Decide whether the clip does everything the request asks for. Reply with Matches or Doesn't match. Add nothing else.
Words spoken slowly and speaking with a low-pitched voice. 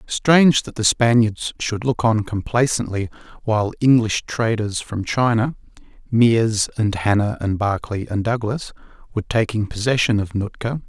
Matches